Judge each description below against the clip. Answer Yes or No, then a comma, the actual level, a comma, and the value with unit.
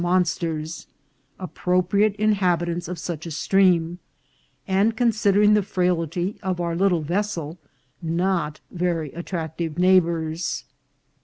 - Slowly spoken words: Yes, slow, 110 wpm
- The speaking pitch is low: No, medium, 175 Hz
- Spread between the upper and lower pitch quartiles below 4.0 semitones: Yes, narrow, 2.5 semitones